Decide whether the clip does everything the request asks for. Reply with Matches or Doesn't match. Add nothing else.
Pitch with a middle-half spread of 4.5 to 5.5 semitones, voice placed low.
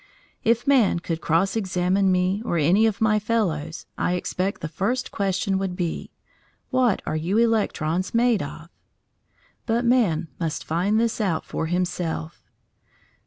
Doesn't match